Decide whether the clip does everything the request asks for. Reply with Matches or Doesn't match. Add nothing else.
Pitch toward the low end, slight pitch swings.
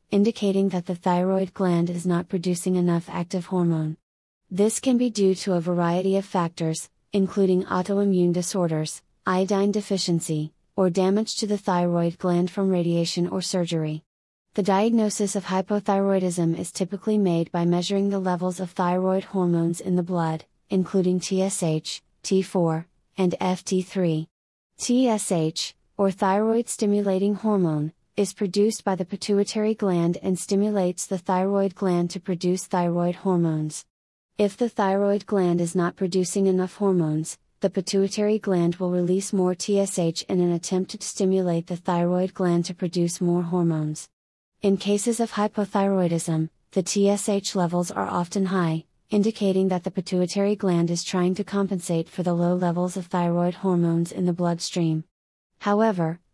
Doesn't match